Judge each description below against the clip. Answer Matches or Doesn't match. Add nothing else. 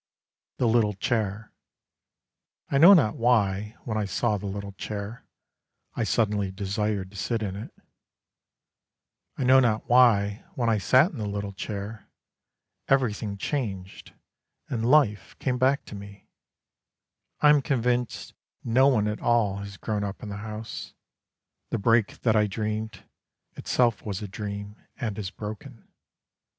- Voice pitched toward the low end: Matches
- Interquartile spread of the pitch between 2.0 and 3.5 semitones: Matches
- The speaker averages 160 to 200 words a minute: Doesn't match